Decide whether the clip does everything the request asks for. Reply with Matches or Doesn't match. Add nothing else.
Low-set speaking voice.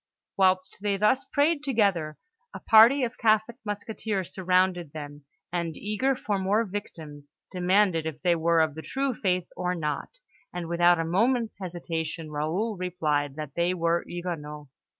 Doesn't match